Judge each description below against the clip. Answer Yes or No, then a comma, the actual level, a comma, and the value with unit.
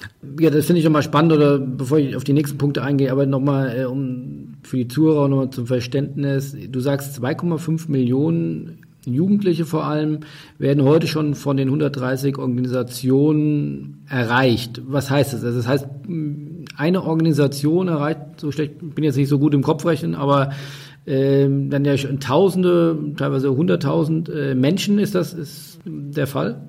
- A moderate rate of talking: Yes, average, 165 wpm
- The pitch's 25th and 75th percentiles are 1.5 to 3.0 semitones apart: Yes, narrow, 2.5 semitones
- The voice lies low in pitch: No, medium, 145 Hz